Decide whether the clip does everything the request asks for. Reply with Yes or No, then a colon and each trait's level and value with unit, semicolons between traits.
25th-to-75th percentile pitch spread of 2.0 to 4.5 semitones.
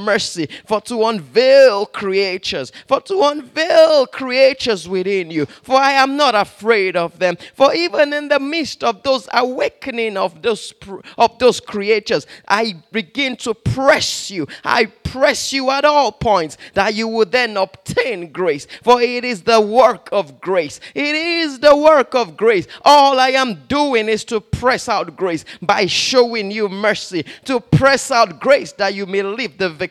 No: wide, 5.4 semitones